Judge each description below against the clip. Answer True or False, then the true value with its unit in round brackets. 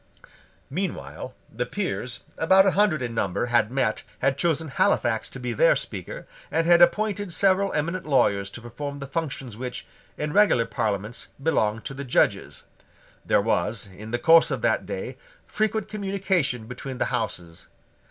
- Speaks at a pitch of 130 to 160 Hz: True (140 Hz)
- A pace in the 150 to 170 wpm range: True (160 wpm)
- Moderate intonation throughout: False (7.9 semitones)